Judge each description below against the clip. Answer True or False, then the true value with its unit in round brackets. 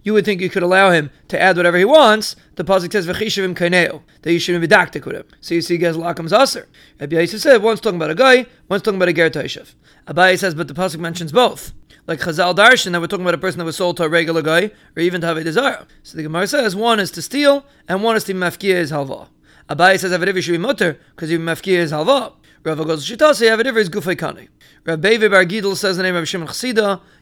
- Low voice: False (185 Hz)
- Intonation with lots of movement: False (3.7 semitones)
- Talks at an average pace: False (245 wpm)